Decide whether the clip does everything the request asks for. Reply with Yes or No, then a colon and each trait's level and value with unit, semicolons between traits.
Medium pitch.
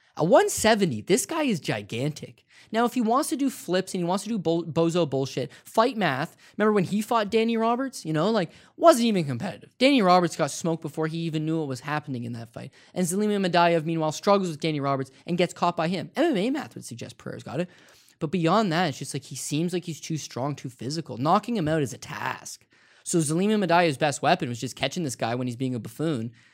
Yes: medium, 165 Hz